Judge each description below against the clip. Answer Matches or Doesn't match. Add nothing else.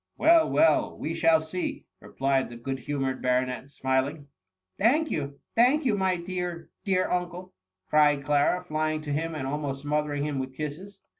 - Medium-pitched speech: Matches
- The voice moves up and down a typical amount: Matches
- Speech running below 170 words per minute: Doesn't match